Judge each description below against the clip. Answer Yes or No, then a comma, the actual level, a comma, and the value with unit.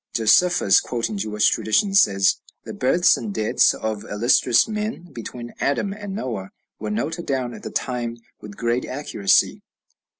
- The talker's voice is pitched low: Yes, low, 120 Hz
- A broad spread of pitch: Yes, wide, 8.2 semitones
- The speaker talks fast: No, average, 145 wpm